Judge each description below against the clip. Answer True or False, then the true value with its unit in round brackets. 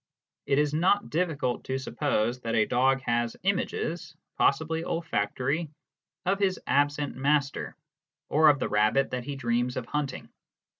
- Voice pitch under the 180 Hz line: True (140 Hz)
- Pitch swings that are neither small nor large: True (4.1 semitones)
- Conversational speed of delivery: True (145 wpm)